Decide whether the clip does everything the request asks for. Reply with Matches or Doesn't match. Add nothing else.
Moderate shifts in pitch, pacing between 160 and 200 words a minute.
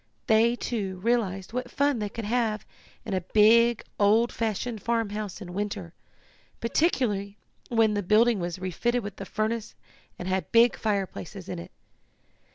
Doesn't match